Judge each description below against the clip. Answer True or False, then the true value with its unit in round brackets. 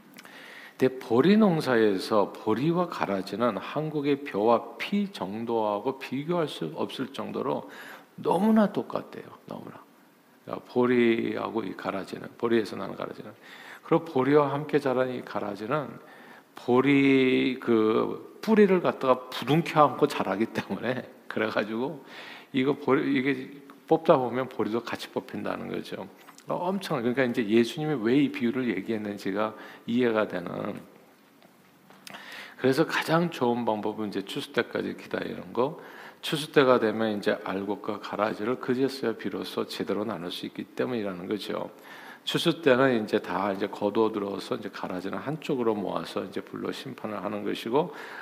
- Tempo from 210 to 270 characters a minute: False (310 characters per minute)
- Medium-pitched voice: False (125 Hz)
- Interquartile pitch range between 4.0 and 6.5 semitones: True (5.4 semitones)